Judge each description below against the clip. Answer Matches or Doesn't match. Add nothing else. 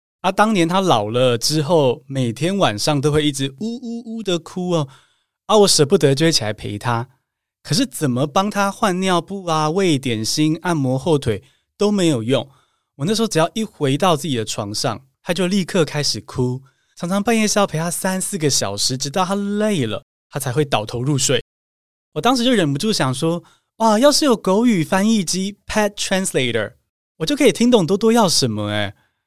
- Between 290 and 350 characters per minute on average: Matches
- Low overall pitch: Doesn't match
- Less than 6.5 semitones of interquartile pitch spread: Doesn't match